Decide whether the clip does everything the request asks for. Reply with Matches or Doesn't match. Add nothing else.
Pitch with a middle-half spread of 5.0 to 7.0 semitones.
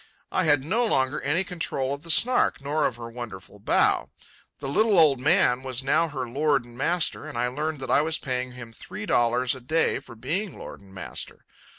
Doesn't match